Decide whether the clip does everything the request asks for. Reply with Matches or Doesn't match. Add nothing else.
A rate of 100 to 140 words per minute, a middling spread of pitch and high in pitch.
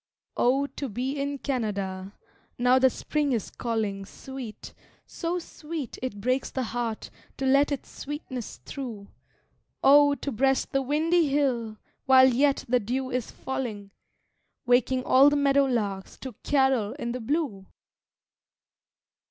Matches